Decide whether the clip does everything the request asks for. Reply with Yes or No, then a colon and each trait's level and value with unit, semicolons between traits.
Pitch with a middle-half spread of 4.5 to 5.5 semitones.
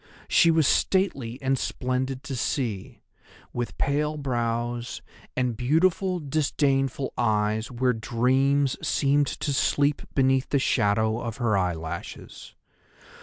No: average, 3.2 semitones